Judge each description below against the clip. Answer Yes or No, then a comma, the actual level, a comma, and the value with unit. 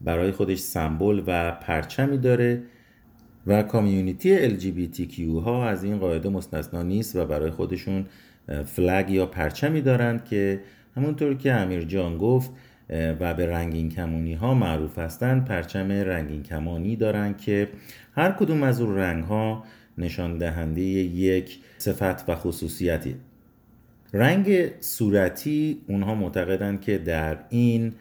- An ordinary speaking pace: Yes, average, 135 wpm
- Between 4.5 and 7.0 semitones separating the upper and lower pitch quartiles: Yes, average, 5.1 semitones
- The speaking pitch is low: Yes, low, 100 Hz